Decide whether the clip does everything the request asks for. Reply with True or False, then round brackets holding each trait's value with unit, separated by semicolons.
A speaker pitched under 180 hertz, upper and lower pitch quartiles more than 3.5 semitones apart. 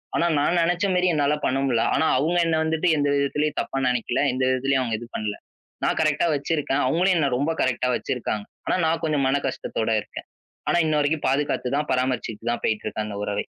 True (140 Hz; 4.0 semitones)